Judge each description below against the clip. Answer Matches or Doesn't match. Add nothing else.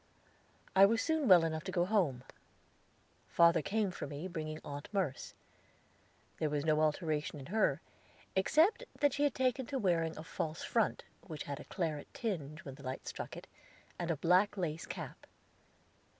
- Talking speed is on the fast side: Doesn't match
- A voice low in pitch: Doesn't match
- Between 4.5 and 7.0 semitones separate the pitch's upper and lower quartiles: Matches